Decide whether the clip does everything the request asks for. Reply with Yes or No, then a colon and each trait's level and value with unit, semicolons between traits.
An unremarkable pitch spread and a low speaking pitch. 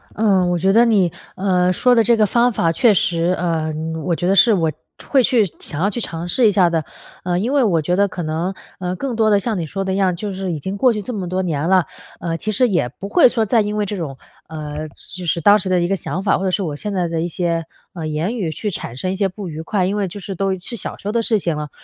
No: average, 3.7 semitones; medium, 185 Hz